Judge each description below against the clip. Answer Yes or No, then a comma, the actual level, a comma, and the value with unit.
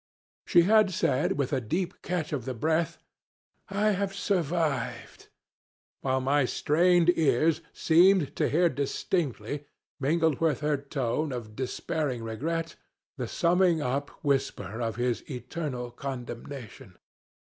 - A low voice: No, medium, 145 Hz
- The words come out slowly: Yes, slow, 125 wpm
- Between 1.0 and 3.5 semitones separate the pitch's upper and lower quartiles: No, average, 4.9 semitones